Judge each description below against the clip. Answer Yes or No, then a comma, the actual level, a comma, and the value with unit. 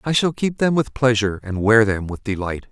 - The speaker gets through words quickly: Yes, fast, 245 wpm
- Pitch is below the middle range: Yes, low, 115 Hz